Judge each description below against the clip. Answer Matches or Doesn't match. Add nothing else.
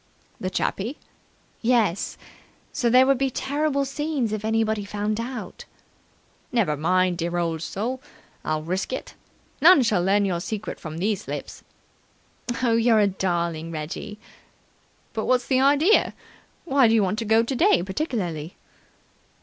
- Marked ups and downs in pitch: Matches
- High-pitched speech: Matches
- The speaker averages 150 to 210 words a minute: Doesn't match